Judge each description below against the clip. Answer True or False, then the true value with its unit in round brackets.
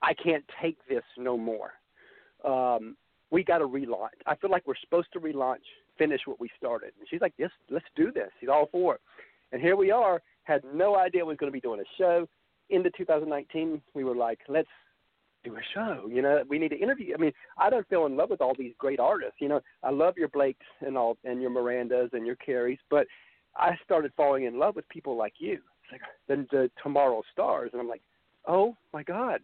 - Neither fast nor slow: False (230 wpm)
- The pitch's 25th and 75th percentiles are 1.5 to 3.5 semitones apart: False (5.3 semitones)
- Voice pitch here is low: False (145 Hz)